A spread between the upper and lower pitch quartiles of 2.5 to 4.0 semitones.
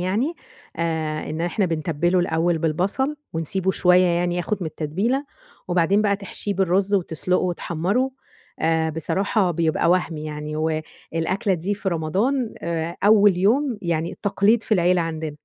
Yes: average, 3.6 semitones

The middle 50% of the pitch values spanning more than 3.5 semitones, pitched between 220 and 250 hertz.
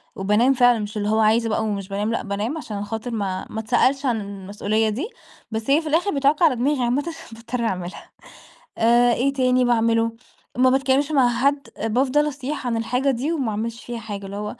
Yes: average, 3.9 semitones; high, 235 Hz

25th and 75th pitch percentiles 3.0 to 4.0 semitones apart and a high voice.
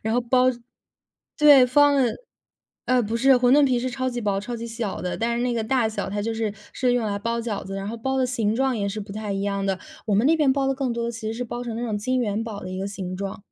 Yes: average, 3.5 semitones; high, 230 Hz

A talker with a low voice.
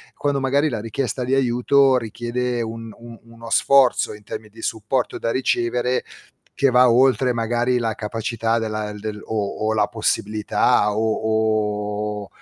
Yes: low, 115 Hz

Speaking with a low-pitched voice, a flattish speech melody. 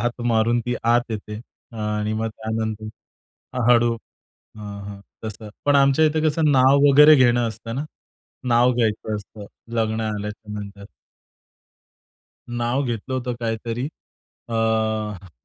Yes: low, 115 Hz; narrow, 2.2 semitones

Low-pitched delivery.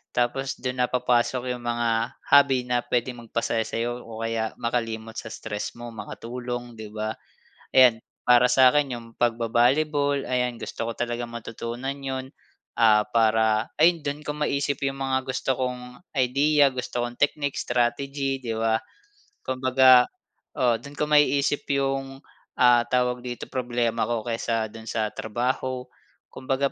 Yes: low, 125 Hz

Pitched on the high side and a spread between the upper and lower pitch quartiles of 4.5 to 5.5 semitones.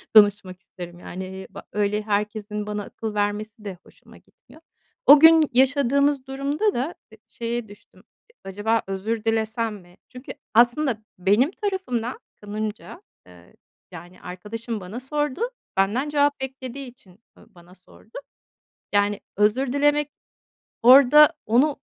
Yes: high, 225 Hz; average, 5.0 semitones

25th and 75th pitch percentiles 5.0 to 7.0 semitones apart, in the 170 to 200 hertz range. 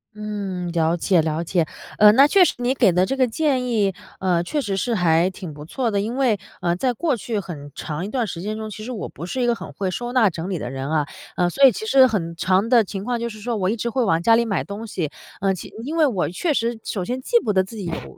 No: average, 5.3 semitones; high, 210 Hz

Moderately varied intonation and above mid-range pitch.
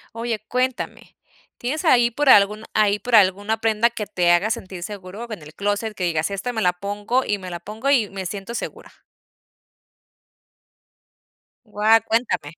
Yes: average, 3.2 semitones; high, 210 Hz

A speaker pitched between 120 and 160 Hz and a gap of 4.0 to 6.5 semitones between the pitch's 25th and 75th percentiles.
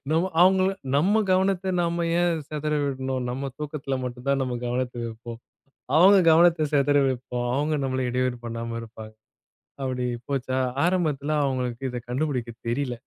Yes: low, 135 Hz; average, 4.3 semitones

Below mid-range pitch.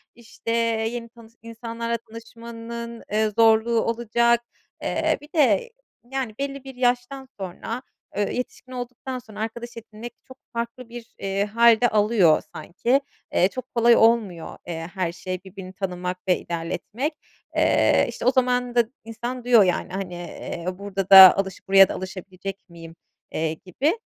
No: high, 230 Hz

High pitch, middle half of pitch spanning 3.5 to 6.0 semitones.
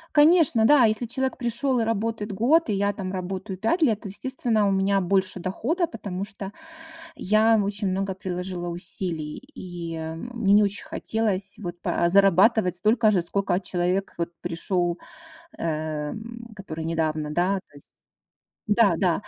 Yes: high, 195 Hz; average, 3.8 semitones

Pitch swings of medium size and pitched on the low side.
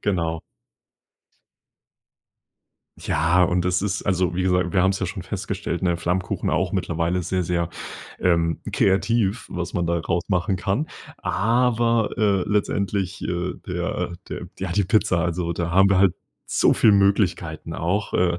No: narrow, 2.2 semitones; very low, 90 Hz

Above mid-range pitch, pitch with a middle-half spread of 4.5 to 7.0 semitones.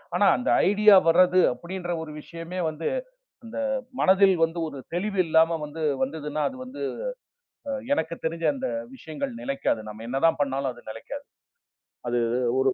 No: medium, 165 Hz; average, 5.2 semitones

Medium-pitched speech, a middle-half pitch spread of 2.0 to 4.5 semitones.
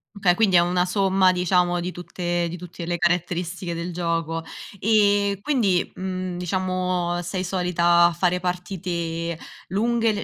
No: medium, 180 Hz; narrow, 1.5 semitones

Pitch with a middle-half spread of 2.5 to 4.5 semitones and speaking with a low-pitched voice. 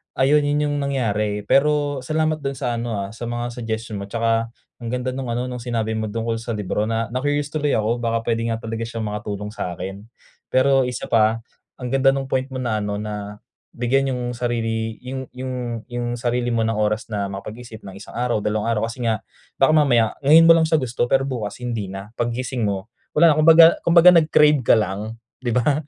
Yes: average, 3.5 semitones; low, 120 Hz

